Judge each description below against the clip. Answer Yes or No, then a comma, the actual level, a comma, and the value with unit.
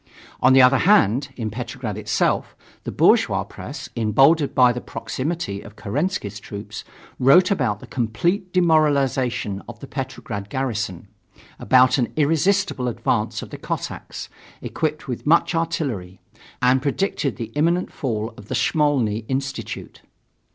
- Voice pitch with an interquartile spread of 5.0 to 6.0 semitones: Yes, wide, 5.6 semitones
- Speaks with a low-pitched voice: Yes, low, 130 Hz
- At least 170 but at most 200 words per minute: No, slow, 135 wpm